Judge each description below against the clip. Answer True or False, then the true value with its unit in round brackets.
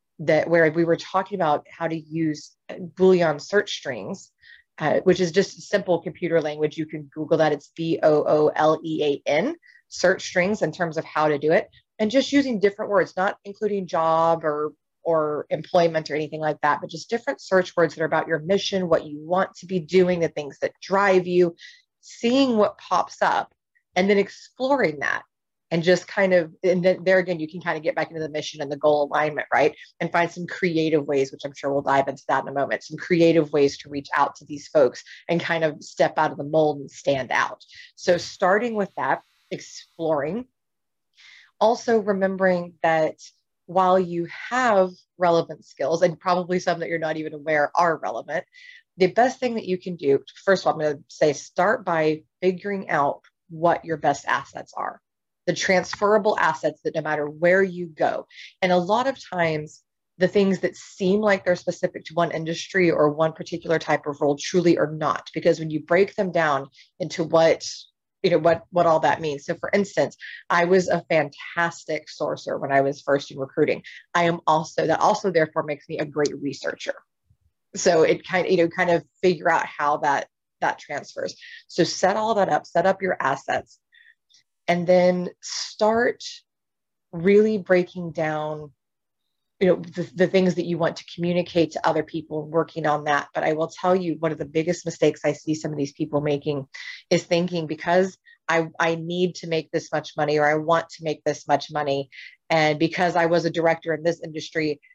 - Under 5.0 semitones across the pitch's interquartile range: True (3.2 semitones)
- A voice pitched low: False (165 Hz)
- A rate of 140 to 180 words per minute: False (200 wpm)